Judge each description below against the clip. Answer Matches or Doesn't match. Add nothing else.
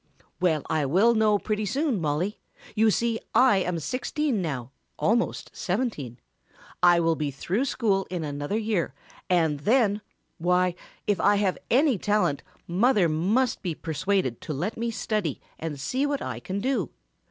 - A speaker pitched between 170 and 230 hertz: Matches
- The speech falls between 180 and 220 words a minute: Doesn't match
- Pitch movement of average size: Doesn't match